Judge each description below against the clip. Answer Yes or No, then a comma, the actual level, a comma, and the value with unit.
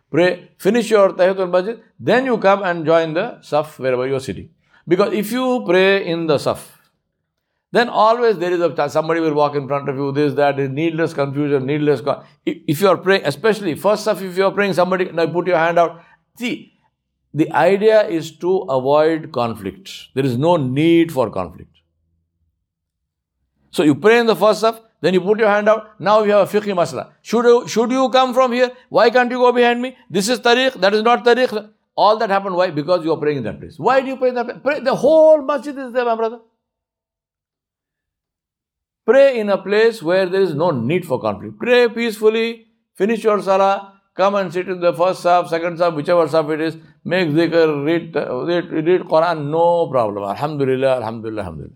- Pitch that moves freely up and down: Yes, wide, 6.6 semitones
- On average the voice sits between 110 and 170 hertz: No, medium, 180 Hz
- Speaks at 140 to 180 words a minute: No, fast, 205 wpm